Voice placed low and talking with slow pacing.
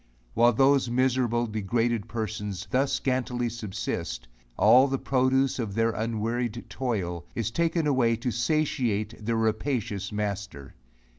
Yes: low, 115 Hz; slow, 125 wpm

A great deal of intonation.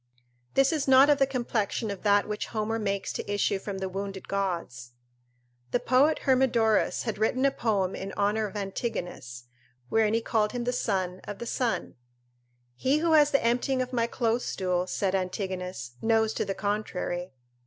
No: average, 4.3 semitones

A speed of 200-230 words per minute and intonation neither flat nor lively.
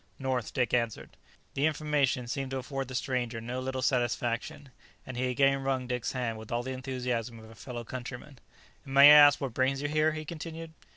No: fast, 205 wpm; narrow, 2.2 semitones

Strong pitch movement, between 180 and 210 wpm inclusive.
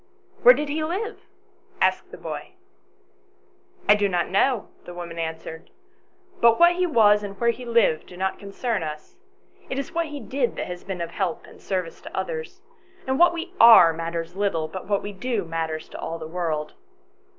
Yes: wide, 7.9 semitones; fast, 205 wpm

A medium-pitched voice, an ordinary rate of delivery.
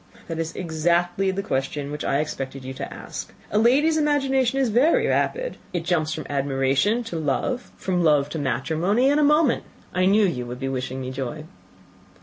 Yes: medium, 170 Hz; average, 185 wpm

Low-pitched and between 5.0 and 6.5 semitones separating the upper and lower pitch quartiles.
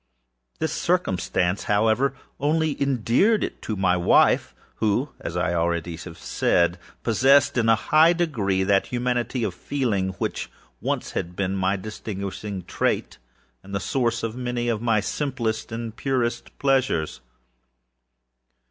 Yes: low, 115 Hz; wide, 5.6 semitones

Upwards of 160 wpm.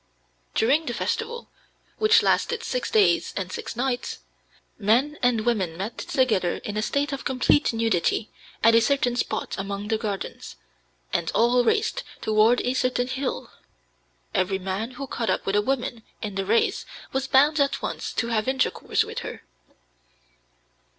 No: average, 155 wpm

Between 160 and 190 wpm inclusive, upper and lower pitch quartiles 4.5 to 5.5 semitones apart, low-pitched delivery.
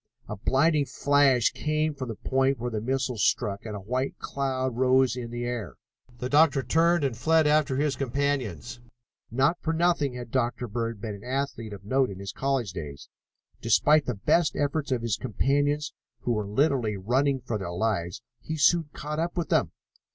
No: average, 185 wpm; average, 4.1 semitones; low, 130 Hz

